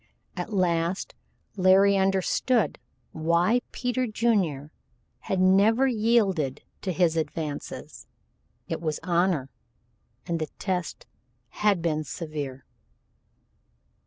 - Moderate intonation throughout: Yes, average, 4.1 semitones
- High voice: No, medium, 180 Hz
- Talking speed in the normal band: No, slow, 95 wpm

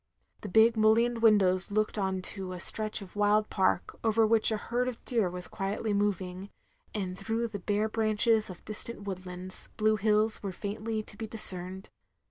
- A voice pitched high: Yes, high, 210 Hz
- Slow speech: No, average, 175 wpm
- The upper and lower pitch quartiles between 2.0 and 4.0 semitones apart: Yes, narrow, 2.5 semitones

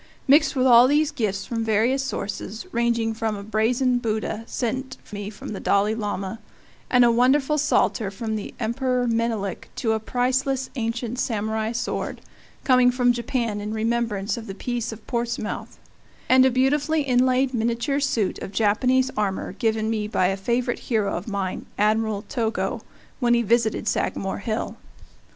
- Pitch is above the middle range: Yes, high, 230 Hz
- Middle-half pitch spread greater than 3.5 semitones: No, average, 2.8 semitones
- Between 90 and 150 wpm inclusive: No, average, 165 wpm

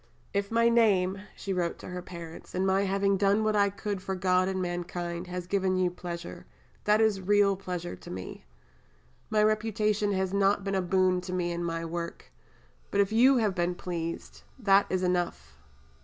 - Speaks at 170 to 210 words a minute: Yes, average, 185 wpm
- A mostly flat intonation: Yes, narrow, 2.3 semitones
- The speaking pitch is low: No, high, 190 Hz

